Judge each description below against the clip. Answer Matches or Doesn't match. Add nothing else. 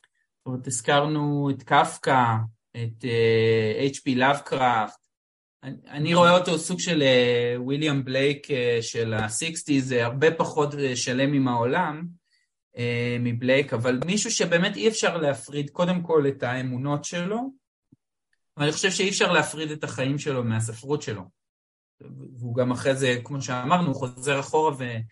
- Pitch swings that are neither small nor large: Matches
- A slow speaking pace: Doesn't match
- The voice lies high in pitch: Doesn't match